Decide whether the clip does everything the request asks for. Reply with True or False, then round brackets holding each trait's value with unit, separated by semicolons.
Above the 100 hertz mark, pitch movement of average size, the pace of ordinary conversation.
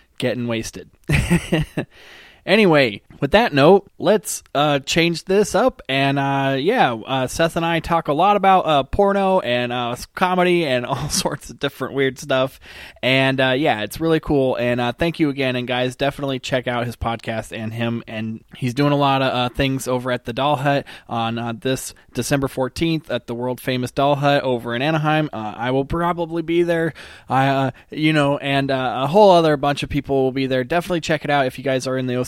False (135 Hz; 4.4 semitones; 210 wpm)